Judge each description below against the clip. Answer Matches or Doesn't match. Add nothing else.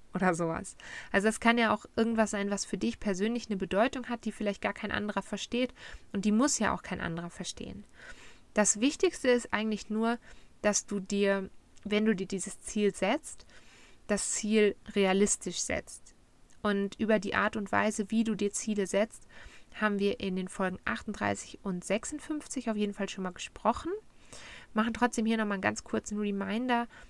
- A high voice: Matches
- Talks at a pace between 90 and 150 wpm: Doesn't match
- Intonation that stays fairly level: Matches